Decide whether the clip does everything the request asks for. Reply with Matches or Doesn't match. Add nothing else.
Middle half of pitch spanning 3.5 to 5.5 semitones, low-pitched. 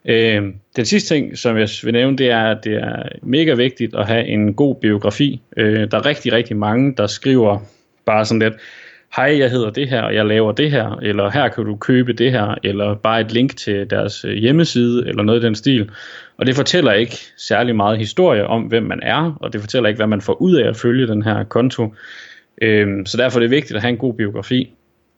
Doesn't match